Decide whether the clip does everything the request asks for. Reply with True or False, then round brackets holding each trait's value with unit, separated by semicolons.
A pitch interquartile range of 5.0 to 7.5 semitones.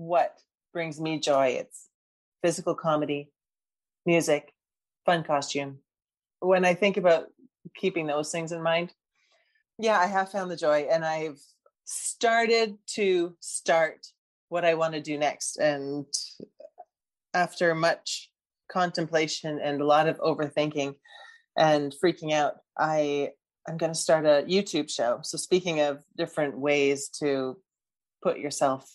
False (3.2 semitones)